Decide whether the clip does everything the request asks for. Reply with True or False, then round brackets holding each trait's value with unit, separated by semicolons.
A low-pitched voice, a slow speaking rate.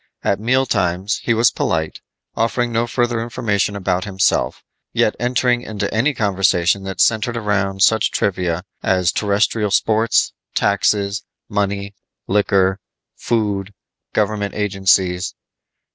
True (100 Hz; 115 wpm)